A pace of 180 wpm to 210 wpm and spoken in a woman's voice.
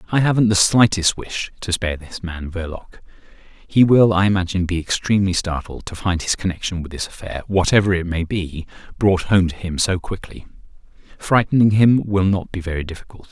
No: average, 185 wpm; male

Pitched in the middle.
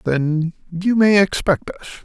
Yes: medium, 180 Hz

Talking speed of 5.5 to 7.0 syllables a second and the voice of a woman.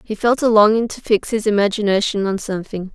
Yes: 6.0 syllables/s; female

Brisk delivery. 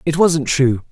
No: average, 195 wpm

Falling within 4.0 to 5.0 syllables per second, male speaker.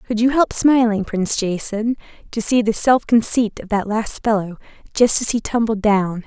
No: 4.9 syllables/s; female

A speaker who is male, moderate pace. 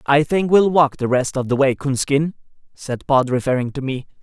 No: male; fast, 215 wpm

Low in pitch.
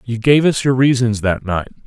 Yes: low, 120 Hz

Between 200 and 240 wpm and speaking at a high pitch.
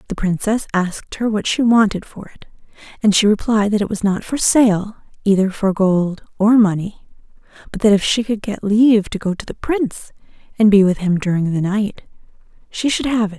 Yes: fast, 205 wpm; high, 205 Hz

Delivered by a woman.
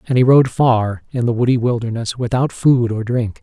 No: male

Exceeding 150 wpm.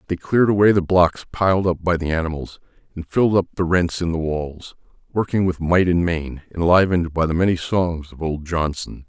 Yes: fast, 205 wpm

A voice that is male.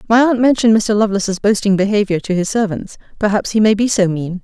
No: female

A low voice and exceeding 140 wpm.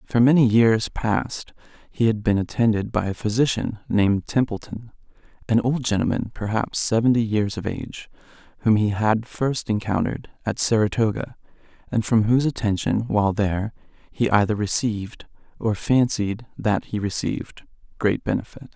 No: low, 110 Hz; slow, 135 wpm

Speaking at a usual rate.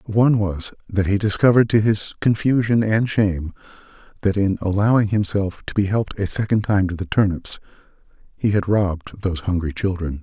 Yes: average, 170 wpm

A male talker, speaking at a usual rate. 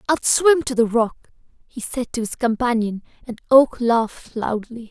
No: female; average, 170 wpm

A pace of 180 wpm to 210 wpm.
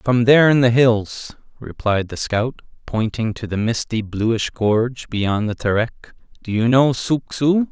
No: average, 170 wpm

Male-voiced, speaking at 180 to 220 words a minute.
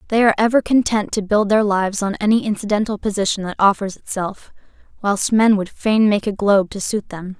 No: female; fast, 205 wpm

